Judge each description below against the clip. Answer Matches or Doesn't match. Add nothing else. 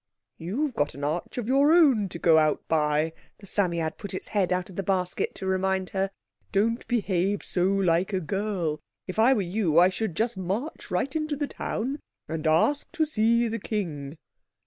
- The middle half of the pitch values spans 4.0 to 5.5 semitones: Matches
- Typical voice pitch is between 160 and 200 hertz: Matches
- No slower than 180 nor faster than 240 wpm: Matches